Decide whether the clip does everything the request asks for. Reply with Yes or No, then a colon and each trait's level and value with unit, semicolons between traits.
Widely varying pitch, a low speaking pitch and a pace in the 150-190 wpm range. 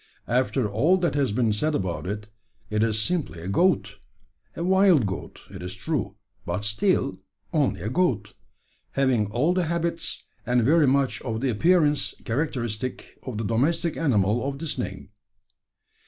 Yes: wide, 7.1 semitones; low, 125 Hz; average, 155 wpm